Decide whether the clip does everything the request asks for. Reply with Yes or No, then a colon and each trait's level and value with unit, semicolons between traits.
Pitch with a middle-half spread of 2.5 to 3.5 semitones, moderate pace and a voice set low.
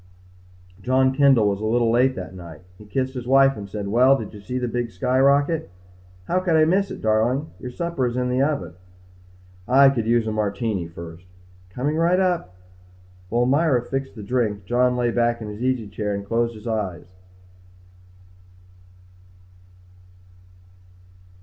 No: average, 4.1 semitones; average, 165 wpm; low, 120 Hz